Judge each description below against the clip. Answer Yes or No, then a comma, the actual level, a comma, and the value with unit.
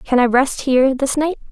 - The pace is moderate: No, fast, 240 wpm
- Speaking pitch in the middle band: No, very high, 270 Hz